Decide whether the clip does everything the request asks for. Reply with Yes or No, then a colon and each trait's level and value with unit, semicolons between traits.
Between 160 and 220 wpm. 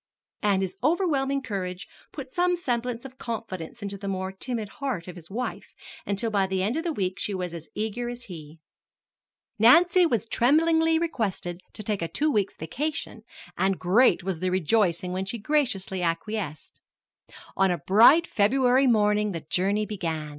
Yes: average, 170 wpm